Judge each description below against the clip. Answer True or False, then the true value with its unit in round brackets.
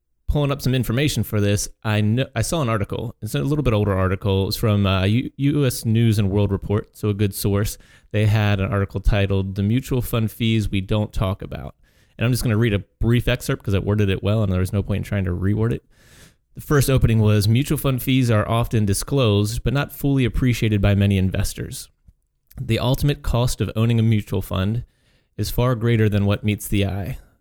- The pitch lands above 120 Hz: False (110 Hz)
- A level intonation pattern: False (3.3 semitones)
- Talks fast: True (220 wpm)